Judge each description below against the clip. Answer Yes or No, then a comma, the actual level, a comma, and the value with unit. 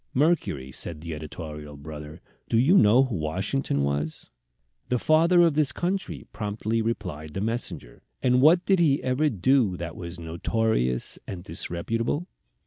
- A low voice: Yes, low, 105 Hz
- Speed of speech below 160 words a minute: Yes, average, 145 wpm